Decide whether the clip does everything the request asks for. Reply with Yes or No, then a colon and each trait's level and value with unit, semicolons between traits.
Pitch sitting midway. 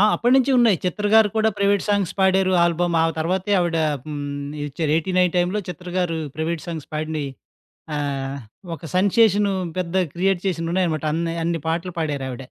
Yes: medium, 175 Hz